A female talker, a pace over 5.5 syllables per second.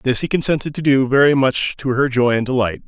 No: male; 5.8 syllables/s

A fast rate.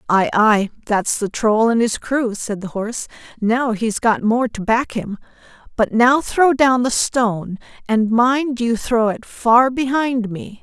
No: average, 180 wpm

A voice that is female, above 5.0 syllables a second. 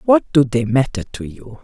No: female; 4.6 syllables/s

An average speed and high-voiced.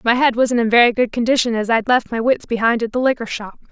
No: fast, 275 wpm; high, 235 Hz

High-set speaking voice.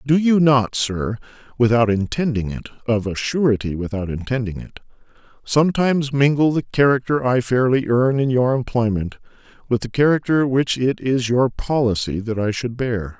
No: low, 125 Hz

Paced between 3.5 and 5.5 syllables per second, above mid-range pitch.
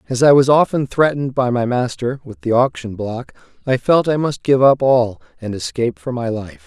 No: 5.3 syllables/s; low, 125 Hz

